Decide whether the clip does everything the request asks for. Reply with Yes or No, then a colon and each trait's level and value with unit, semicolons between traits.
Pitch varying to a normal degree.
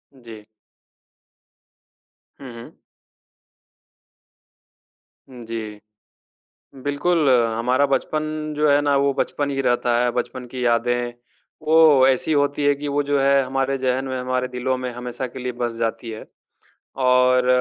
No: narrow, 2.3 semitones